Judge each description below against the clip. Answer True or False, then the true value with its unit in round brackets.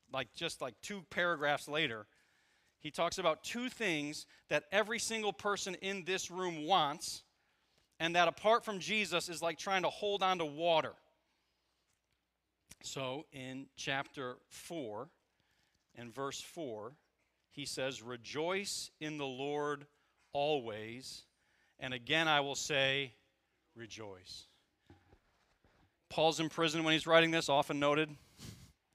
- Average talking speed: False (125 wpm)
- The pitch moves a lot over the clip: False (4.3 semitones)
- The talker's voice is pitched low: False (155 Hz)